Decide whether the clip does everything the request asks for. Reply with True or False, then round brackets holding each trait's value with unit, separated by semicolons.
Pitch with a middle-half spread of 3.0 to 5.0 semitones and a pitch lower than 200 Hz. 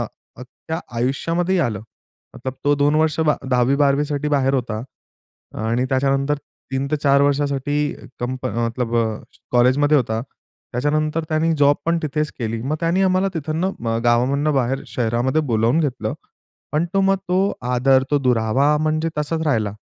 True (3.5 semitones; 140 Hz)